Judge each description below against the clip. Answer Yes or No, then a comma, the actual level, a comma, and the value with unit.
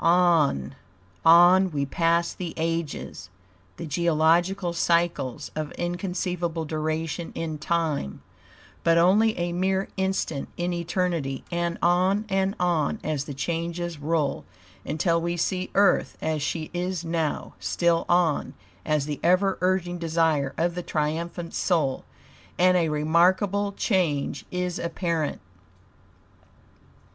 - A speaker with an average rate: No, slow, 120 wpm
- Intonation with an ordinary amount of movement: No, narrow, 2.2 semitones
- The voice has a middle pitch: Yes, medium, 170 Hz